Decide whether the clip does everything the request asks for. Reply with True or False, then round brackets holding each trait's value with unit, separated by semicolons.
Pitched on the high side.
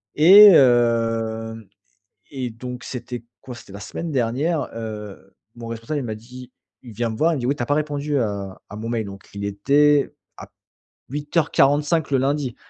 False (125 Hz)